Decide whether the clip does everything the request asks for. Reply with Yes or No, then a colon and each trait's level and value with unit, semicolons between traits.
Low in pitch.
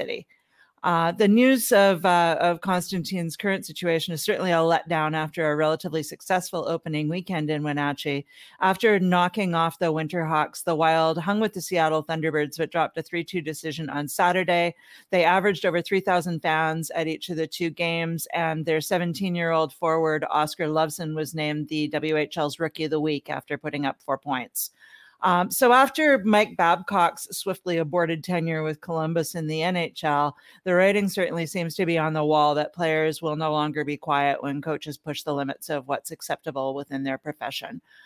No: medium, 165 Hz